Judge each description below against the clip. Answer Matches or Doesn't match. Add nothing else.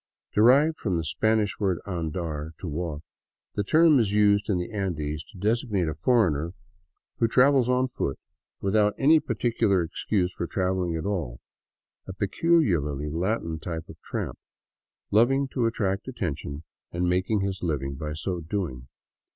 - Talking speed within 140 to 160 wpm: Matches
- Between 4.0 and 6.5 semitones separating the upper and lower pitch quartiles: Matches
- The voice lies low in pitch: Matches